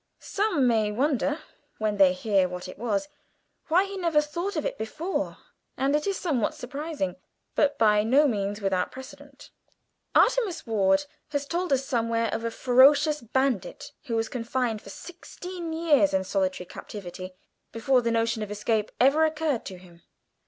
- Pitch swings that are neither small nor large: No, wide, 6.3 semitones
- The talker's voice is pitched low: No, high, 245 Hz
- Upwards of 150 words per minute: Yes, average, 160 wpm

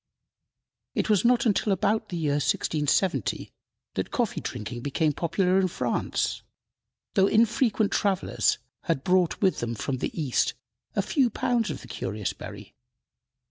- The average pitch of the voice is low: No, medium, 185 Hz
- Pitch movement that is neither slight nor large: No, wide, 6.5 semitones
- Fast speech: No, average, 140 wpm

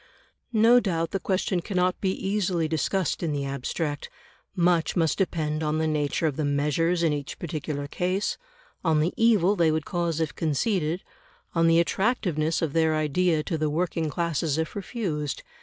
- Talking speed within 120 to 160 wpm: No, average, 170 wpm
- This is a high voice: No, medium, 165 Hz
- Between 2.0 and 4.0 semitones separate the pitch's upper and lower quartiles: Yes, average, 3.0 semitones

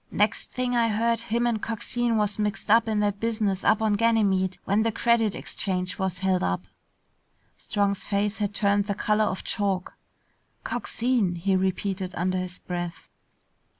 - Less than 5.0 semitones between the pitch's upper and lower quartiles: Yes, average, 2.9 semitones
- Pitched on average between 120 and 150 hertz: No, high, 205 Hz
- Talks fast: No, average, 160 wpm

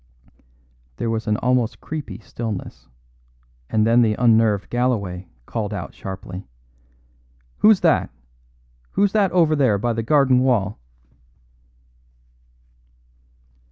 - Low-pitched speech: Yes, low, 115 Hz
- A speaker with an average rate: No, slow, 105 wpm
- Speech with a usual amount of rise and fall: Yes, average, 3.5 semitones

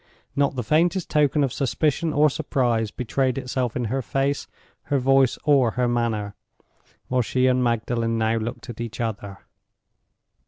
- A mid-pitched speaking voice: No, low, 125 Hz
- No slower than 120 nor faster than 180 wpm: Yes, average, 155 wpm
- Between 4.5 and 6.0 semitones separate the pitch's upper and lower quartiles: No, average, 3.1 semitones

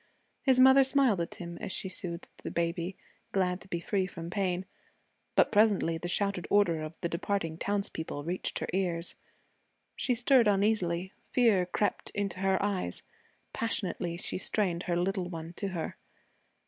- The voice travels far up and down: No, average, 3.1 semitones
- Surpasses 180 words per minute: No, average, 160 wpm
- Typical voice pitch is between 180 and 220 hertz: Yes, medium, 185 Hz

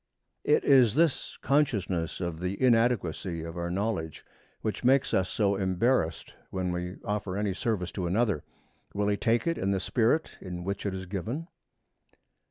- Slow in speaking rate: No, average, 165 wpm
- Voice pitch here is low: Yes, low, 100 Hz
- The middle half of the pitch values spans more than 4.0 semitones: Yes, average, 4.6 semitones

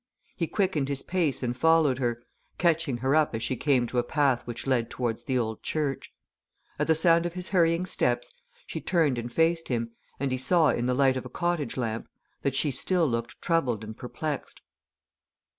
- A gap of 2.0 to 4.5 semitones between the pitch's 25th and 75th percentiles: No, average, 5.2 semitones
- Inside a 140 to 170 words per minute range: No, average, 195 wpm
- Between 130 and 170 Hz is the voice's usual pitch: Yes, low, 135 Hz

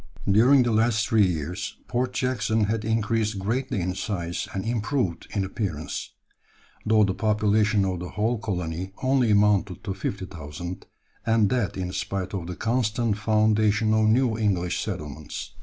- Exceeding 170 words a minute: No, average, 150 wpm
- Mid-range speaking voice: No, low, 105 Hz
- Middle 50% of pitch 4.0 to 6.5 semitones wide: No, average, 3.1 semitones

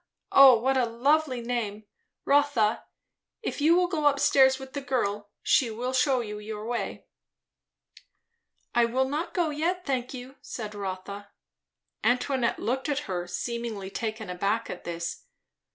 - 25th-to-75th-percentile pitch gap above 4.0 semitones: Yes, average, 4.4 semitones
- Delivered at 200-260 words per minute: No, average, 150 wpm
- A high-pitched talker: Yes, high, 245 Hz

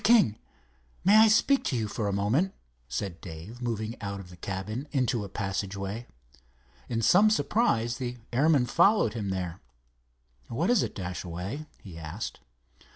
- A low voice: Yes, low, 110 Hz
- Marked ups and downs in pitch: Yes, wide, 6.8 semitones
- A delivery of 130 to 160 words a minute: Yes, average, 155 wpm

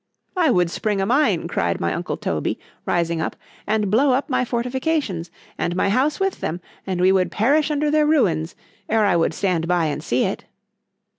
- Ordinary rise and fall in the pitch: No, wide, 8.0 semitones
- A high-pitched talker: Yes, high, 210 Hz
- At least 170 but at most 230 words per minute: Yes, average, 190 wpm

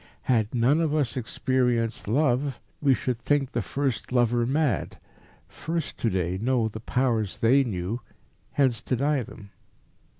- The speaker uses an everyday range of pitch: Yes, average, 3.4 semitones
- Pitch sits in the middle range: No, low, 125 Hz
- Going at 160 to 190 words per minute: No, average, 140 wpm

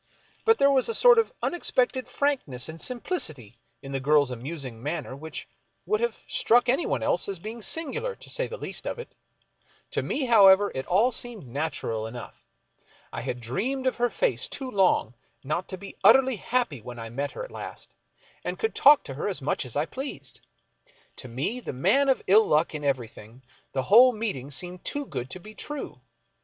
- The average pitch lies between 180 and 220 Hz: Yes, high, 190 Hz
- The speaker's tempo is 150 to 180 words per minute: No, average, 195 wpm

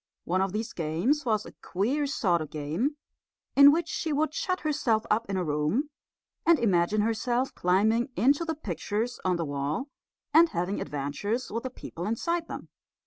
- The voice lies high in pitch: Yes, high, 220 Hz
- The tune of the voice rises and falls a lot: Yes, wide, 8.1 semitones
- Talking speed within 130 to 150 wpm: No, average, 175 wpm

